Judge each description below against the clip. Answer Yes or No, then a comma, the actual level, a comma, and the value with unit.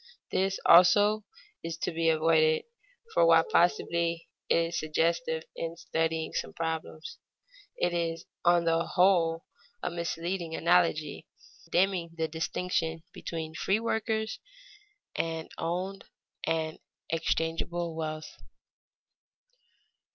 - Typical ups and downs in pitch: No, narrow, 1.3 semitones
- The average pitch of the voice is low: No, medium, 165 Hz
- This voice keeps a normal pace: No, slow, 105 wpm